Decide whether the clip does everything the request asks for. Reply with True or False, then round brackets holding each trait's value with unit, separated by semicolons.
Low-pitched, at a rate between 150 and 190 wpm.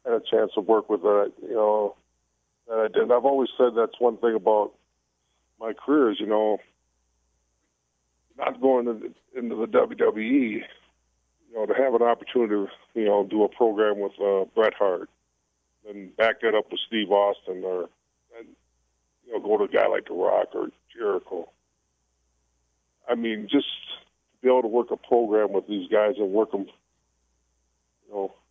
True (100 Hz; 180 wpm)